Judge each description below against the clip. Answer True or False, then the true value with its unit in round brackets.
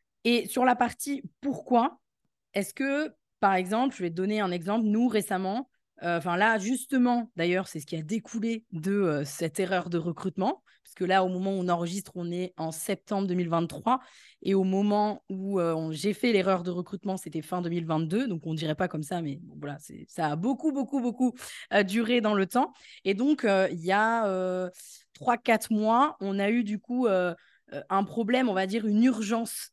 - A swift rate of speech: False (205 wpm)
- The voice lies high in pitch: True (200 Hz)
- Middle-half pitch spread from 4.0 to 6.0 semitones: True (4.4 semitones)